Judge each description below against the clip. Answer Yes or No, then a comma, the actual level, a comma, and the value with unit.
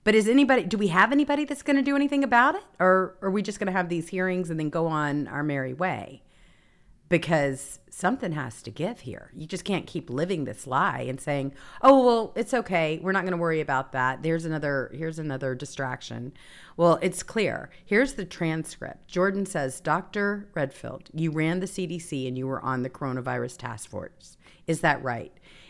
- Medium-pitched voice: Yes, medium, 165 Hz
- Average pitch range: No, wide, 6.0 semitones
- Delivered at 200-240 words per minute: Yes, fast, 205 wpm